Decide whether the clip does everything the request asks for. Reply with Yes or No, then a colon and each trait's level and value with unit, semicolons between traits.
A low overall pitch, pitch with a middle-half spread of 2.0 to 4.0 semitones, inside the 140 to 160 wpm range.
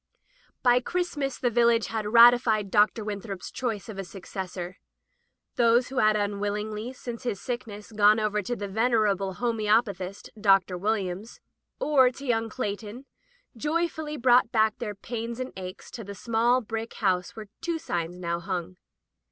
No: high, 220 Hz; average, 3.2 semitones; average, 150 wpm